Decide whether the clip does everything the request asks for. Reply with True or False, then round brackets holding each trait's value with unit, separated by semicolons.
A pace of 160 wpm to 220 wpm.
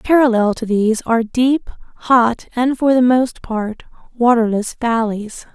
False (140 wpm)